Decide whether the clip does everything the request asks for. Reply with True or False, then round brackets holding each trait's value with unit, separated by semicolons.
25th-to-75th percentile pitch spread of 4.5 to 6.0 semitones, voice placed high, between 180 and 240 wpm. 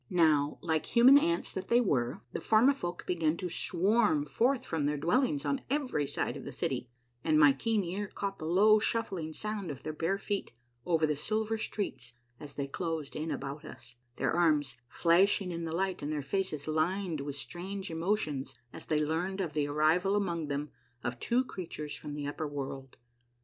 False (5.1 semitones; 165 Hz; 185 wpm)